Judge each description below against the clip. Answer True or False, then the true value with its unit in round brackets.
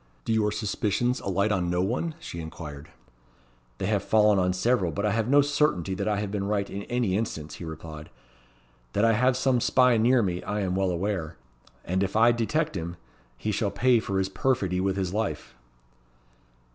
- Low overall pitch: True (100 Hz)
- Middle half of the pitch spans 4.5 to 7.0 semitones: False (3.8 semitones)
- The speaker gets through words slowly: False (195 wpm)